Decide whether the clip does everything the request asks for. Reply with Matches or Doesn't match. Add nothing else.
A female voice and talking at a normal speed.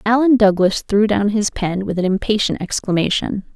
Matches